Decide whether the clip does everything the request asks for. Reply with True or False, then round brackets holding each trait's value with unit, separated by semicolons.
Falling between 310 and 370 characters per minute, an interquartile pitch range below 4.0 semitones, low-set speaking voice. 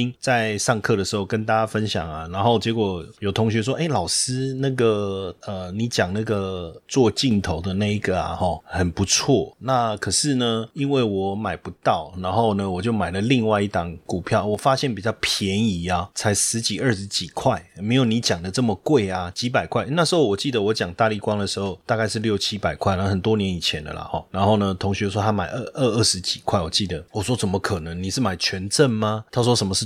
True (315 characters per minute; 3.0 semitones; 105 Hz)